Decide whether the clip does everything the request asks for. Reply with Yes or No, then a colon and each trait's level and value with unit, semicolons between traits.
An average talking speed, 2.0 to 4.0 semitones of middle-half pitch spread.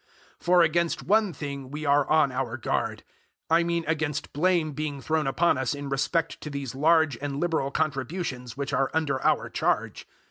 Yes: average, 180 wpm; average, 3.1 semitones